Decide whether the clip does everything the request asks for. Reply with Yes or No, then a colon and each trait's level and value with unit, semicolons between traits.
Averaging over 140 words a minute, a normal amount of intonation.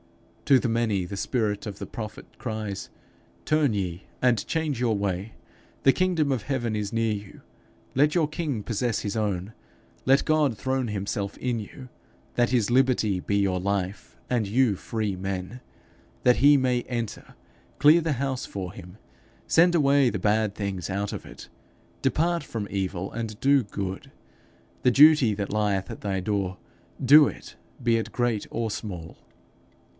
Yes: average, 160 wpm; average, 4.8 semitones